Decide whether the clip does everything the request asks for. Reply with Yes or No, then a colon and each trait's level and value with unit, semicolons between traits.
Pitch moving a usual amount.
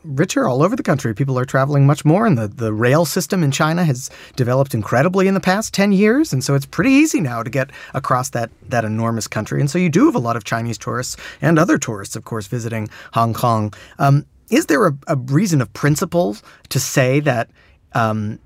No: wide, 5.7 semitones